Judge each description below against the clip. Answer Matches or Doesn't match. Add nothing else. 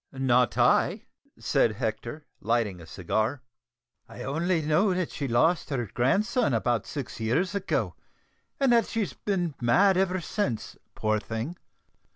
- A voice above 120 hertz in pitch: Matches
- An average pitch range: Doesn't match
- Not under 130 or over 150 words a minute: Matches